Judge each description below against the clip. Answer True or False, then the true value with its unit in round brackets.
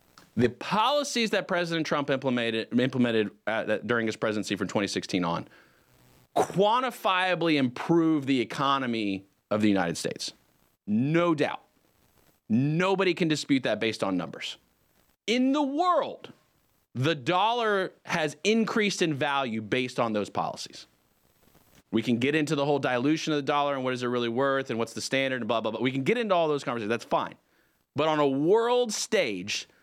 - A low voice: False (145 Hz)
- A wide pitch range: True (7.0 semitones)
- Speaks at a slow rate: False (165 wpm)